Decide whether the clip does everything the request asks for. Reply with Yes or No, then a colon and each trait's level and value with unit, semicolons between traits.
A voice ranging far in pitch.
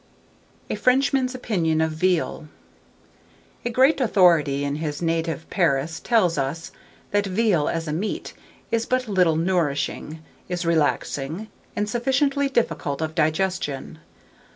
Yes: wide, 6.2 semitones